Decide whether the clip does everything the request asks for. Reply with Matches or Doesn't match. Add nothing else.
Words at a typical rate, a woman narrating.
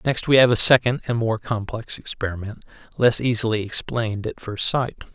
Doesn't match